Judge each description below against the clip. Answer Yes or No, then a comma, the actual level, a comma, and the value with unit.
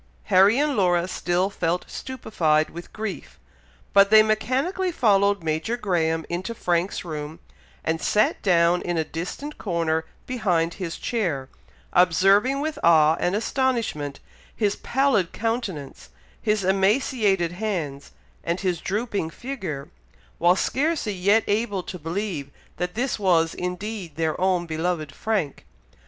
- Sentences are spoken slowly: Yes, slow, 130 wpm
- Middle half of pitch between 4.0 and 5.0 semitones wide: Yes, average, 4.7 semitones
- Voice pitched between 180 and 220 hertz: Yes, medium, 185 Hz